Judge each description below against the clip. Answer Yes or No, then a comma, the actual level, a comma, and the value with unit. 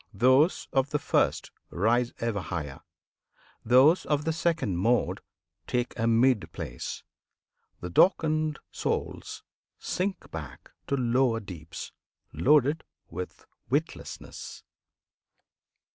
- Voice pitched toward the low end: Yes, low, 125 Hz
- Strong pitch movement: Yes, wide, 5.7 semitones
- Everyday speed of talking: No, slow, 100 wpm